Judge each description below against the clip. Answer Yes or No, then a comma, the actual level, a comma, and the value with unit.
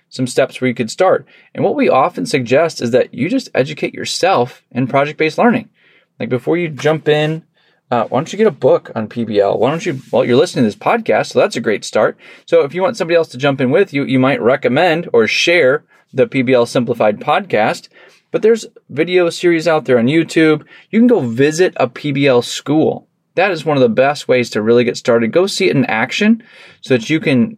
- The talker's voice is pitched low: No, medium, 155 Hz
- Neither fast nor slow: No, fast, 225 wpm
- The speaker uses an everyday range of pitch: No, wide, 6.9 semitones